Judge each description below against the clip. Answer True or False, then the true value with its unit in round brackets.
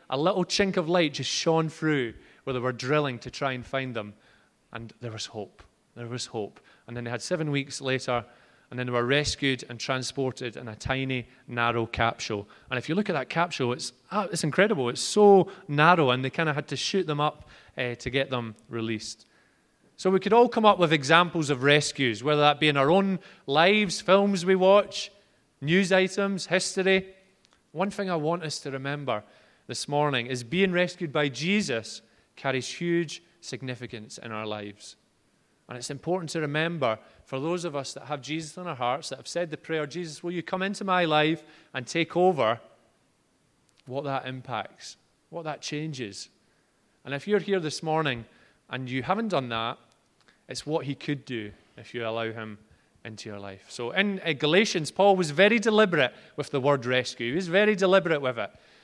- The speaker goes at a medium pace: True (195 wpm)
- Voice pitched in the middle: True (145 Hz)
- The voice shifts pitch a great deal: True (6.3 semitones)